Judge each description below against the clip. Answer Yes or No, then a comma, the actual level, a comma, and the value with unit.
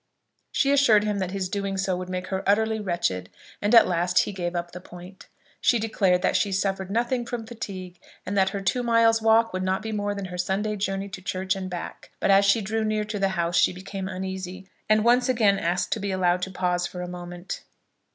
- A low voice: No, high, 195 Hz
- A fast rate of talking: Yes, fast, 225 wpm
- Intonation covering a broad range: No, average, 2.8 semitones